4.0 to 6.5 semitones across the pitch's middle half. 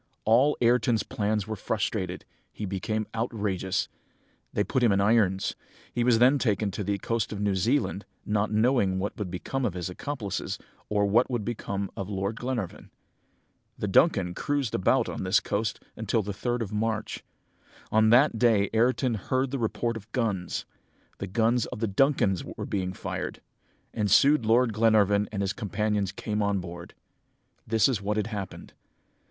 No: average, 2.9 semitones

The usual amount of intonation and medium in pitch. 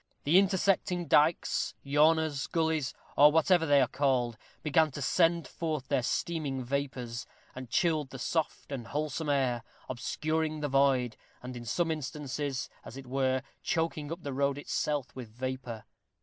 Yes: average, 3.5 semitones; medium, 145 Hz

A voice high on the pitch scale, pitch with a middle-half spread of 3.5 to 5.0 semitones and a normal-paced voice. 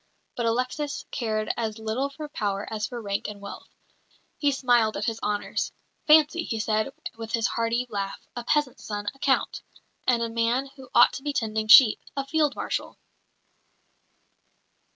Yes: high, 235 Hz; average, 3.9 semitones; average, 165 wpm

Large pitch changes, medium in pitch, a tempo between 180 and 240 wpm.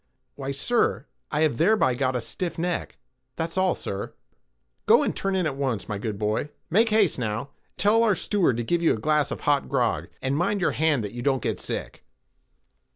Yes: wide, 6.6 semitones; medium, 145 Hz; average, 190 wpm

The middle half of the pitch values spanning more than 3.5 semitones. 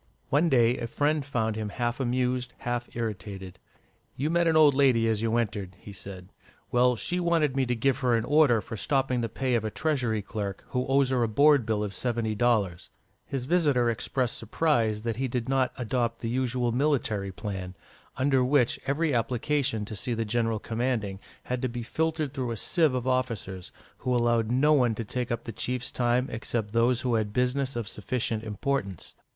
No: average, 3.0 semitones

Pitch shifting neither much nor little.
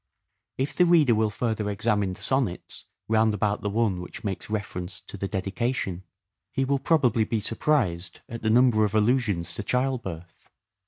Yes: average, 4.0 semitones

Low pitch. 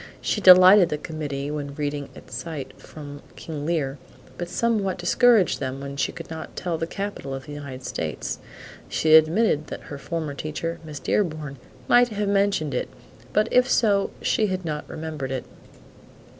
No: medium, 155 Hz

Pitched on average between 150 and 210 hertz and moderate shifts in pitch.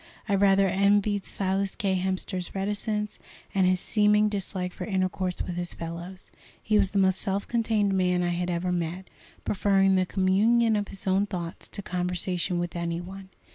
No: high, 190 Hz; narrow, 2.0 semitones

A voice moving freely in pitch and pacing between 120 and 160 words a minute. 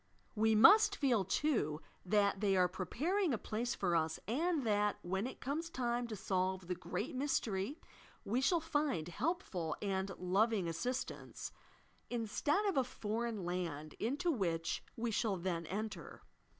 Yes: wide, 6.3 semitones; average, 150 wpm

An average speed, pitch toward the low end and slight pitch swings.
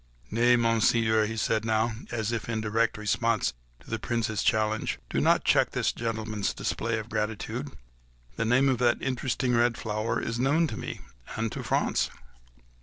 Yes: average, 175 wpm; low, 115 Hz; narrow, 1.4 semitones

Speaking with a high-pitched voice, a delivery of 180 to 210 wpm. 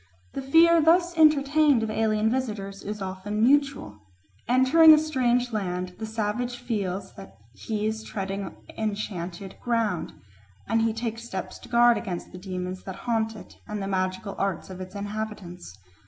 No: high, 215 Hz; average, 155 wpm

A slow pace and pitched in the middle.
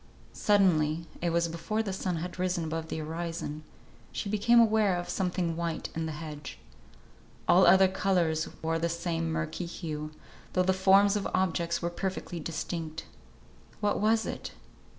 No: average, 155 wpm; medium, 170 Hz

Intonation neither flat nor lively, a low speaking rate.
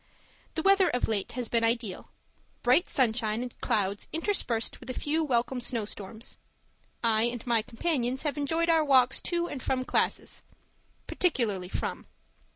No: average, 4.7 semitones; average, 155 wpm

